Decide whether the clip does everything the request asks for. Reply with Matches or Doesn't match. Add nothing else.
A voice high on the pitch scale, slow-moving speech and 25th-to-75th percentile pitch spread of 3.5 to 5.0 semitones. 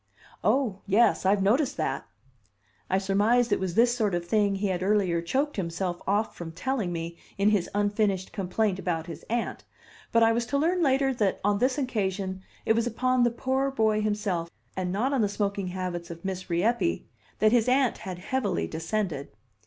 Doesn't match